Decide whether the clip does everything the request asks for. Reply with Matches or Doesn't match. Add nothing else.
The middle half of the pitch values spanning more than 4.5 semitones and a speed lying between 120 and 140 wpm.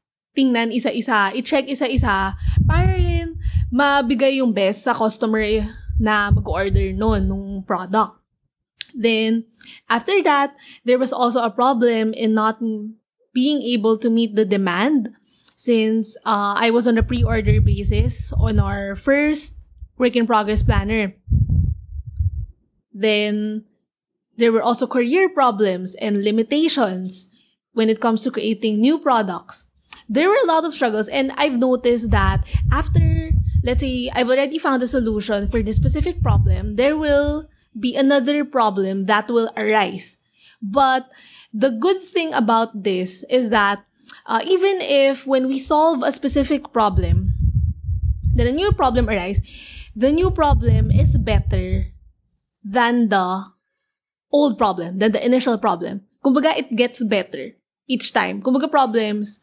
Matches